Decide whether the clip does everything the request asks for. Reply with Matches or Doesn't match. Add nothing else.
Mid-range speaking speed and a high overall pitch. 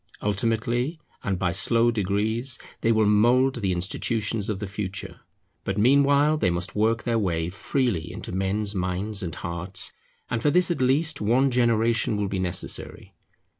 Doesn't match